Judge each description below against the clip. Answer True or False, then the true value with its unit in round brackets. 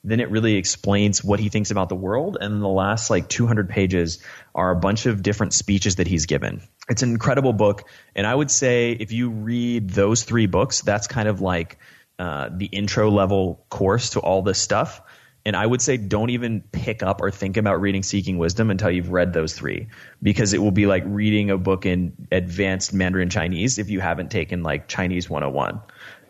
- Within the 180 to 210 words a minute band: True (205 wpm)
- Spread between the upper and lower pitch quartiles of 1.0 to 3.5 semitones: True (3.0 semitones)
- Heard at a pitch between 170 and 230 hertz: False (100 Hz)